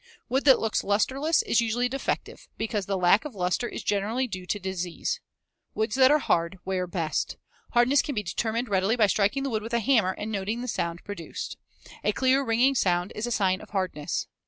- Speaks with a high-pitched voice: Yes, high, 215 Hz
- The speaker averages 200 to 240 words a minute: Yes, fast, 205 wpm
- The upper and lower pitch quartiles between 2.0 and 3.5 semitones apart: No, average, 4.7 semitones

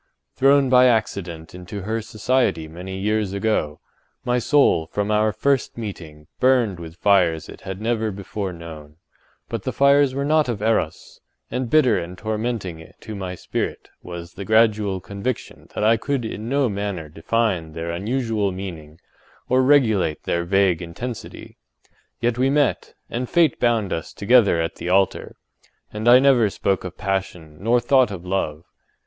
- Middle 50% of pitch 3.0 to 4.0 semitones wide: No, average, 5.3 semitones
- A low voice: Yes, low, 105 Hz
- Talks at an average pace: Yes, average, 160 wpm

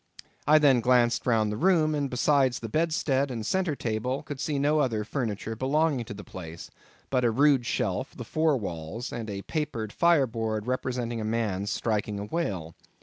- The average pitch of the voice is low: Yes, low, 120 Hz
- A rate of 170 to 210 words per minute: Yes, average, 180 wpm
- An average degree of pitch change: Yes, average, 5.0 semitones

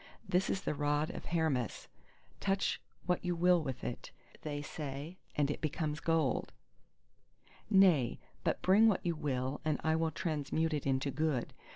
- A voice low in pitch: No, medium, 155 Hz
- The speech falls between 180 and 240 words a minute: No, average, 160 wpm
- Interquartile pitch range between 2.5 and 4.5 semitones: Yes, average, 3.3 semitones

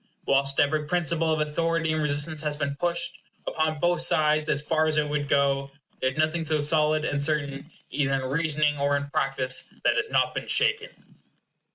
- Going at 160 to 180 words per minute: No, average, 190 wpm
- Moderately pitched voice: Yes, medium, 150 Hz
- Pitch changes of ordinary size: No, narrow, 1.9 semitones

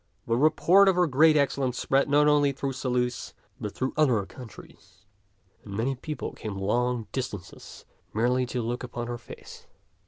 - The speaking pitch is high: No, low, 125 Hz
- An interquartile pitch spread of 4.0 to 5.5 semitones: No, average, 3.4 semitones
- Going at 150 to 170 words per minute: Yes, average, 160 wpm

